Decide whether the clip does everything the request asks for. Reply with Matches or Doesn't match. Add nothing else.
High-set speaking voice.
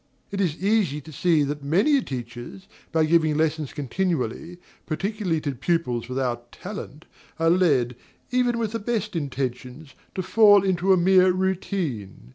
Doesn't match